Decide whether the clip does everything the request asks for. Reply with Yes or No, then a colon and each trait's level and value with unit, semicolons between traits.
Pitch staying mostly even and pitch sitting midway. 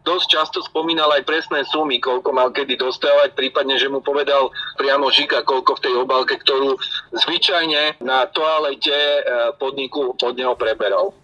No: average, 3.1 semitones; medium, 145 Hz